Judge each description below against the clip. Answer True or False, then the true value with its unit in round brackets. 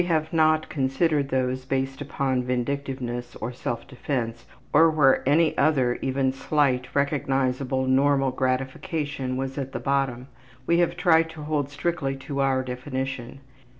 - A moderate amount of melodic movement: False (2.3 semitones)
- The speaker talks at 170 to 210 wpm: False (145 wpm)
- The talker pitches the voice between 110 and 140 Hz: True (135 Hz)